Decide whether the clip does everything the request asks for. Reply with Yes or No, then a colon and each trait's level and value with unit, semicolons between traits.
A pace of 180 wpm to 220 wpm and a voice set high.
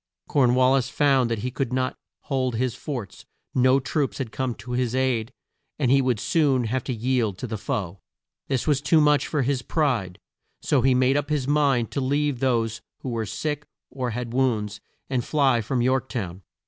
No: average, 200 wpm; low, 130 Hz